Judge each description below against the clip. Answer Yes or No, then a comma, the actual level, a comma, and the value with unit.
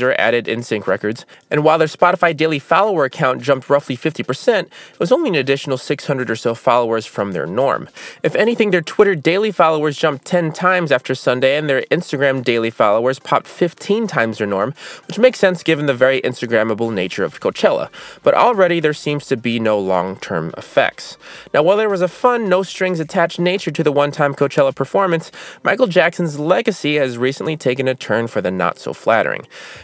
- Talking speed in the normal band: Yes, average, 195 wpm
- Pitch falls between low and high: Yes, medium, 150 Hz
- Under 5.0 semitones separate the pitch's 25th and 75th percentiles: No, wide, 5.6 semitones